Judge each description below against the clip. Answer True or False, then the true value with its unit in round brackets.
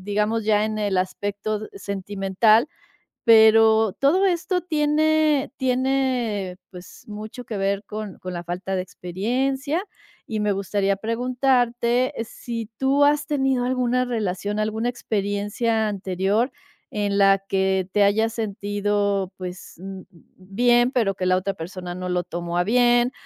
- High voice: True (215 Hz)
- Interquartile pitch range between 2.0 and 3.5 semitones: False (4.0 semitones)